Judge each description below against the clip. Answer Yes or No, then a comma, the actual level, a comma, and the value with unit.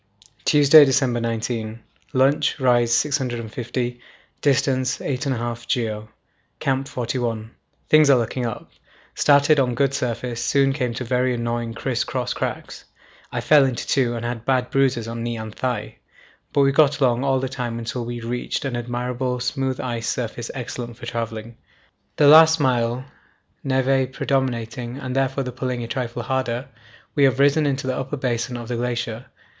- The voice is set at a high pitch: No, low, 125 Hz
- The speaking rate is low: No, average, 160 wpm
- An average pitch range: No, narrow, 2.3 semitones